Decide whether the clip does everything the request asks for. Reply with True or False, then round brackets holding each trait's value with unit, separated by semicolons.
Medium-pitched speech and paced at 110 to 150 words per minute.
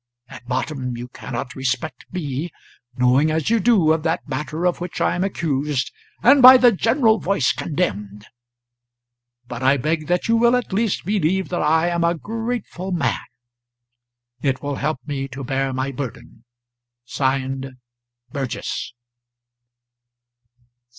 True (155 Hz; 140 wpm)